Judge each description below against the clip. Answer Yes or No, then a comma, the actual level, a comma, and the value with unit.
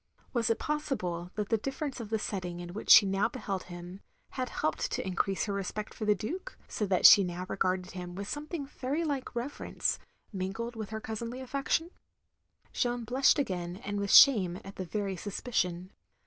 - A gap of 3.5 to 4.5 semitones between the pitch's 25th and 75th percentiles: No, average, 5.3 semitones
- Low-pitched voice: No, high, 210 Hz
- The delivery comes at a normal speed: Yes, average, 190 wpm